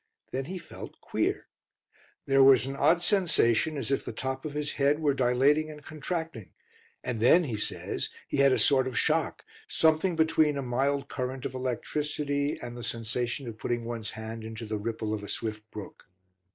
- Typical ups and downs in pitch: Yes, average, 4.2 semitones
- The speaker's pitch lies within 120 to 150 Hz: Yes, low, 135 Hz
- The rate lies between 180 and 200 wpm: Yes, average, 185 wpm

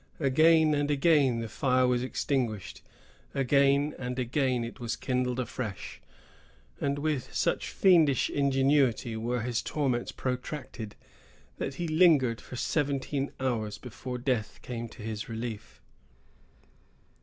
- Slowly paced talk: Yes, slow, 120 wpm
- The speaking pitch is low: Yes, low, 130 Hz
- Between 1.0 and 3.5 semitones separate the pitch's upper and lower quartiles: Yes, average, 3.0 semitones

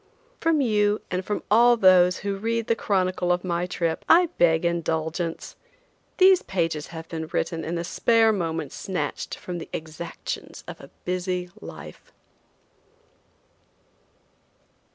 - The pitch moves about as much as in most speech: Yes, average, 3.9 semitones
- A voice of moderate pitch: Yes, medium, 180 Hz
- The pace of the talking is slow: Yes, slow, 130 wpm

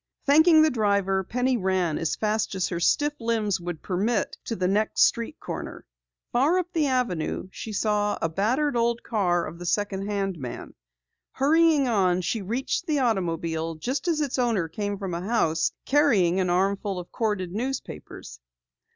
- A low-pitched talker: No, high, 205 Hz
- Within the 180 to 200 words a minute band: No, average, 170 wpm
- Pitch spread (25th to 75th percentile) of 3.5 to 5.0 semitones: No, wide, 5.6 semitones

